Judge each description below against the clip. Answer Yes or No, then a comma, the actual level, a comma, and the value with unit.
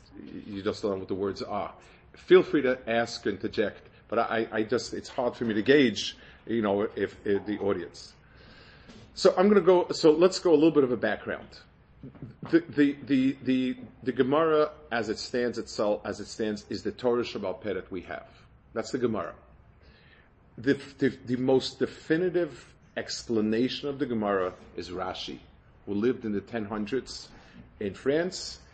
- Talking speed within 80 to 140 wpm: No, average, 180 wpm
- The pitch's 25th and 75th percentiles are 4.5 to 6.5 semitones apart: Yes, average, 5.0 semitones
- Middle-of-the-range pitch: No, low, 125 Hz